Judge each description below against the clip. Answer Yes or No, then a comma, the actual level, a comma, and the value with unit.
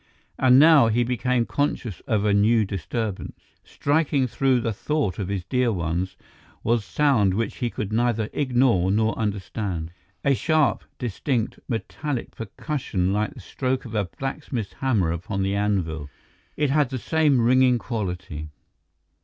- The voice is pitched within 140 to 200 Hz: No, low, 115 Hz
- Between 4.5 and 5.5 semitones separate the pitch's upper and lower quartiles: Yes, average, 4.9 semitones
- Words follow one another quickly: No, average, 145 wpm